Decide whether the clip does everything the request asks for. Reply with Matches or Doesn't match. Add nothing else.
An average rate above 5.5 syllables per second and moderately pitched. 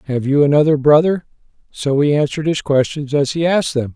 Matches